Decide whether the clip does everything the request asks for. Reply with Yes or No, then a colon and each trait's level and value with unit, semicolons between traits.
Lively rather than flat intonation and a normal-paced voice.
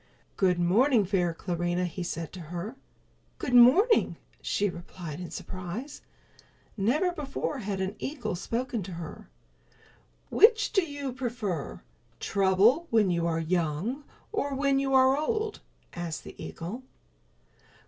No: wide, 7.5 semitones; slow, 130 wpm